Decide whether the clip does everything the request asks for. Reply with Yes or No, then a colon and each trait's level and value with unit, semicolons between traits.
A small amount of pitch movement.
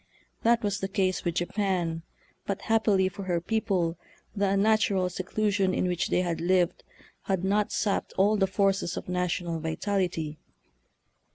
Yes: narrow, 2.3 semitones